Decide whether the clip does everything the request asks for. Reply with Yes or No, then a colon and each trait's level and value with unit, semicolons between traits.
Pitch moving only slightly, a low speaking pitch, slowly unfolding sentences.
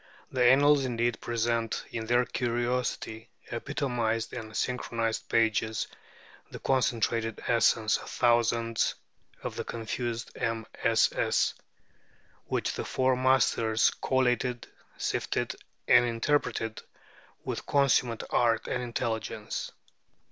Yes: narrow, 1.7 semitones; low, 120 Hz; slow, 95 wpm